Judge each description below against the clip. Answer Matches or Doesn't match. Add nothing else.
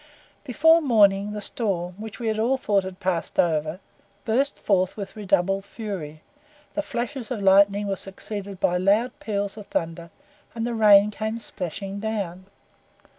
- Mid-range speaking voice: Doesn't match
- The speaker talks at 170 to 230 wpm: Doesn't match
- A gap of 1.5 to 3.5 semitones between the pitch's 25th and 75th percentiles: Matches